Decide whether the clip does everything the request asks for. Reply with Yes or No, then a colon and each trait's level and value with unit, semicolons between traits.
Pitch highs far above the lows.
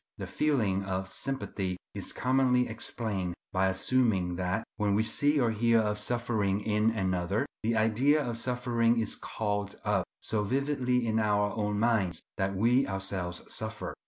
No: average, 3.8 semitones